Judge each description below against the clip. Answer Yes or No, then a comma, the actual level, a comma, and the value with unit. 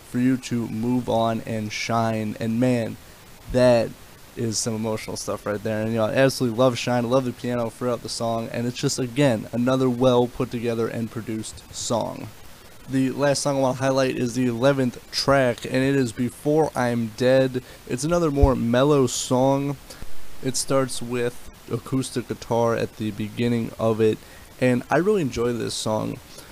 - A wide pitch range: No, narrow, 2.6 semitones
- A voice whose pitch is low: Yes, low, 120 Hz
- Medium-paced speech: Yes, average, 180 wpm